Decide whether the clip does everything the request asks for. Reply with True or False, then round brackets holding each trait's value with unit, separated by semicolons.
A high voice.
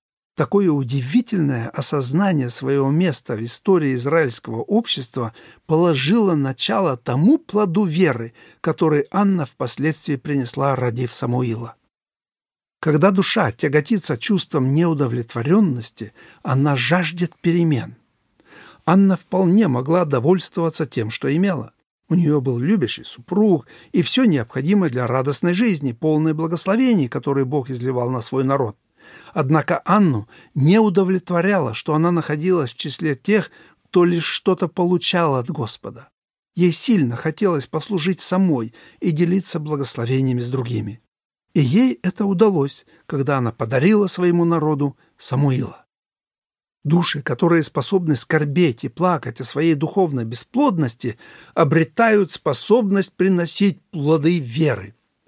False (160 Hz)